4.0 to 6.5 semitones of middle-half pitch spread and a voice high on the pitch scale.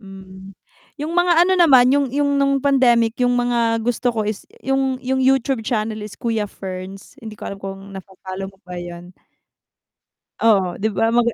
Yes: average, 5.3 semitones; high, 230 Hz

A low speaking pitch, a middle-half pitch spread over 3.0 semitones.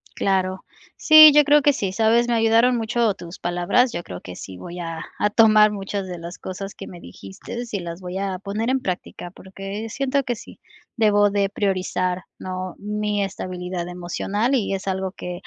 No: high, 195 Hz; average, 3.6 semitones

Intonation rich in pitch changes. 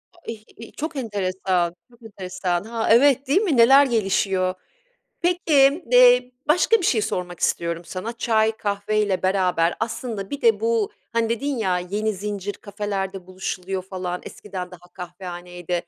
No: average, 4.8 semitones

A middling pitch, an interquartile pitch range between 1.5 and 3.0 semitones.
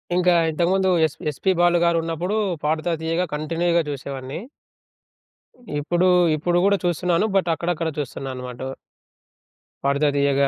No: medium, 165 Hz; average, 3.4 semitones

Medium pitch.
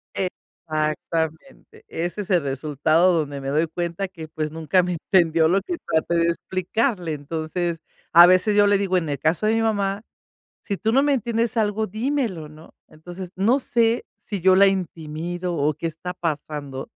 Yes: medium, 175 Hz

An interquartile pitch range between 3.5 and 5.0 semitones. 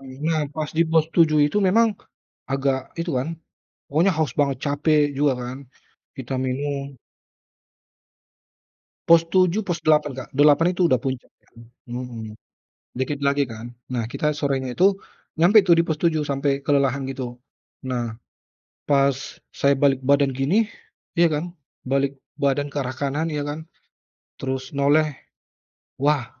No: average, 2.8 semitones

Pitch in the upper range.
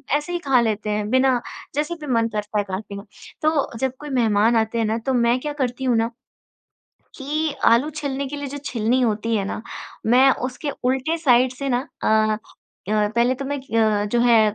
Yes: high, 245 Hz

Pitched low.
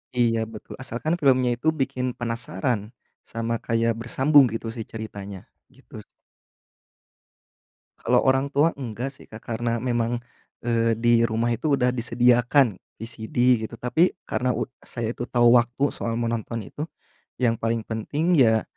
Yes: low, 120 Hz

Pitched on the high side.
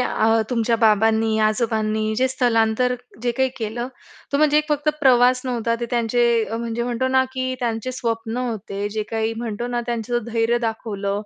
Yes: high, 235 Hz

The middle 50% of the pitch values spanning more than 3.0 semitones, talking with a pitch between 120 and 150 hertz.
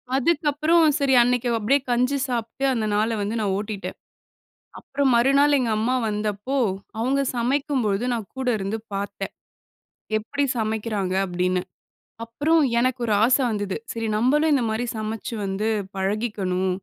No: average, 4.3 semitones; high, 230 Hz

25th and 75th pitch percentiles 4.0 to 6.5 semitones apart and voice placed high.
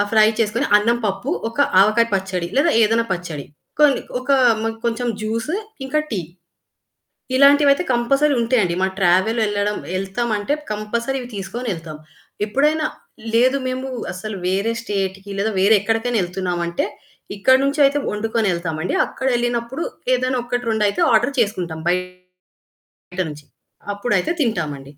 Yes: average, 4.5 semitones; high, 220 Hz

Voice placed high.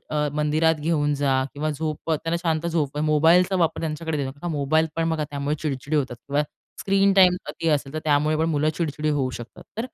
No: medium, 155 Hz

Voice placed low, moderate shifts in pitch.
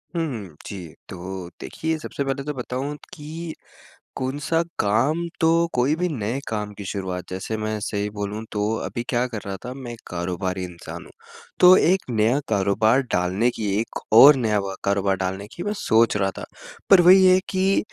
No: low, 110 Hz; wide, 6.9 semitones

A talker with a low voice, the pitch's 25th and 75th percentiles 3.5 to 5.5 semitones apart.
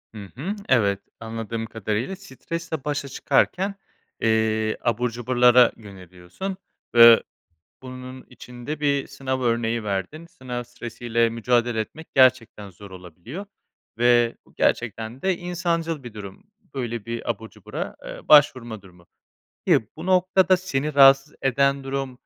Yes: low, 120 Hz; average, 3.9 semitones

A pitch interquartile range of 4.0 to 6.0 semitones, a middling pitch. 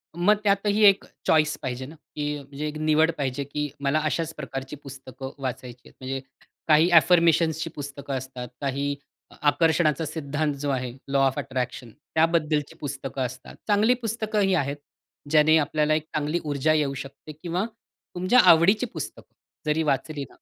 No: average, 3.1 semitones; medium, 150 Hz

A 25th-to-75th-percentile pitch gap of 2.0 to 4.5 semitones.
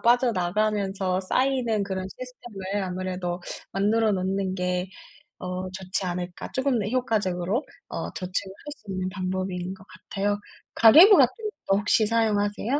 Yes: average, 3.1 semitones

